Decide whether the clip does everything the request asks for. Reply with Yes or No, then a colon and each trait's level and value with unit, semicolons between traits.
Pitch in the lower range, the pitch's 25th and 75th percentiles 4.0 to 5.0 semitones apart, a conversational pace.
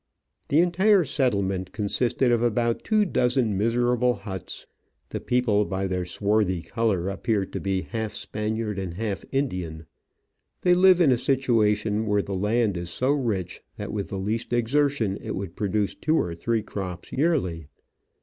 Yes: low, 110 Hz; average, 4.4 semitones; average, 160 wpm